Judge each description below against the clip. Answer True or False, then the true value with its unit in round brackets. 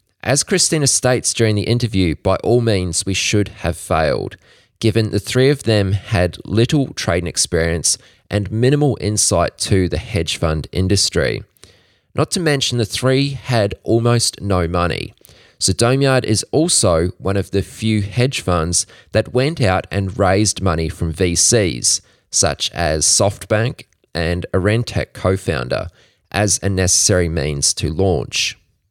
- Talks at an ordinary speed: True (145 wpm)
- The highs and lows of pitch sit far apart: False (4.5 semitones)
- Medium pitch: False (100 Hz)